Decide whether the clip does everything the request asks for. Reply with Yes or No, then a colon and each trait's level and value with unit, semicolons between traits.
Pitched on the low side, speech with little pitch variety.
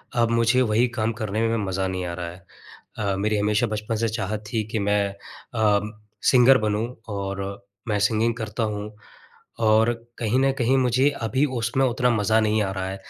Yes: low, 110 Hz; narrow, 2.2 semitones